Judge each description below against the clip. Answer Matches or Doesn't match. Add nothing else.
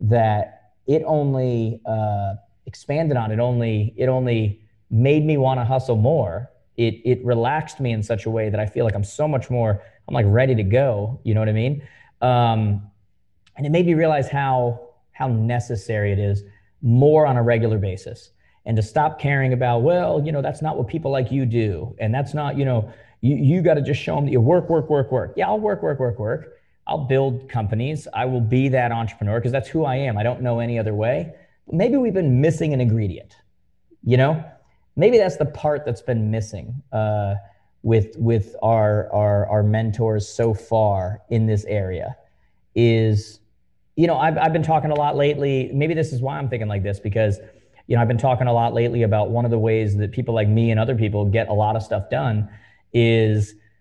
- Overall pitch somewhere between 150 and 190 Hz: Doesn't match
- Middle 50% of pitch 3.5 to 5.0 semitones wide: Matches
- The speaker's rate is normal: Doesn't match